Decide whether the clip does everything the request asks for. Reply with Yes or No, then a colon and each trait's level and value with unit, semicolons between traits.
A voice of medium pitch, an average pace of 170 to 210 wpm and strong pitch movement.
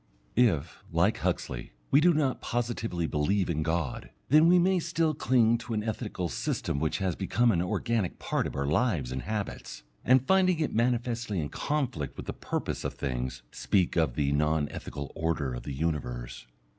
No: very low, 95 Hz; average, 180 wpm; wide, 8.7 semitones